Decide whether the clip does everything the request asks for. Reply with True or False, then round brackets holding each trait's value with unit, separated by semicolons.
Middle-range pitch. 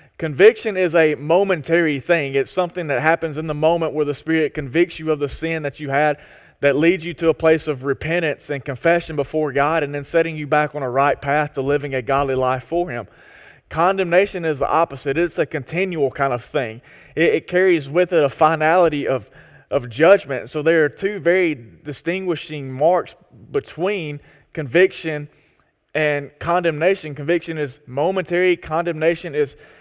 True (155 Hz)